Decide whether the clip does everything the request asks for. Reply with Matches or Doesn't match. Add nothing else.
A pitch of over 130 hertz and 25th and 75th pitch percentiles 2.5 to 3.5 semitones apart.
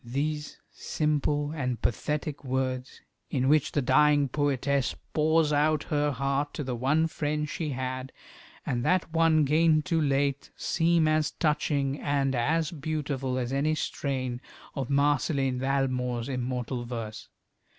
Matches